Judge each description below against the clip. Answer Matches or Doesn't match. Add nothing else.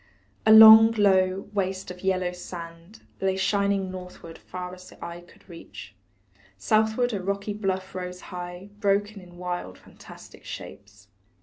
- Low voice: Doesn't match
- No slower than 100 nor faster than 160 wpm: Matches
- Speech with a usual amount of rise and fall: Doesn't match